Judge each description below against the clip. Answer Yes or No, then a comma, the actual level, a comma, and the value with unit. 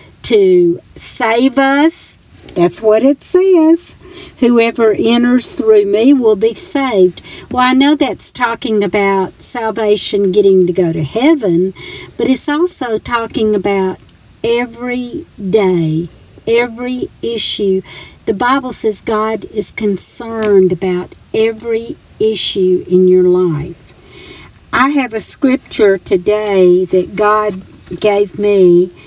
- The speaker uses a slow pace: Yes, slow, 115 wpm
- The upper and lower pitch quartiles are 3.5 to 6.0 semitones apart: Yes, average, 4.5 semitones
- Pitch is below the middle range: No, high, 215 Hz